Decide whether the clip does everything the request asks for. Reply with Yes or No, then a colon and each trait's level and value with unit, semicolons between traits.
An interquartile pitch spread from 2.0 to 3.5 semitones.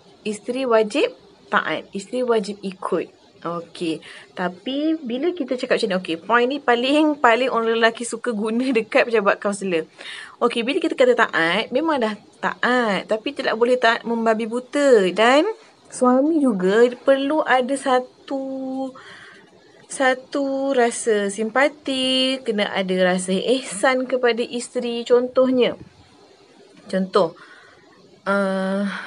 No: average, 4.0 semitones